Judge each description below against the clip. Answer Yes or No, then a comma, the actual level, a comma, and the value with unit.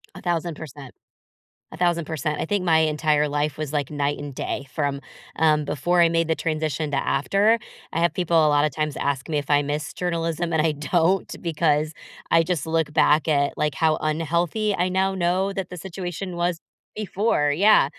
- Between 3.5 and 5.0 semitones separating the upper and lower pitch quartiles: No, average, 2.9 semitones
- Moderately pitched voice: Yes, medium, 160 Hz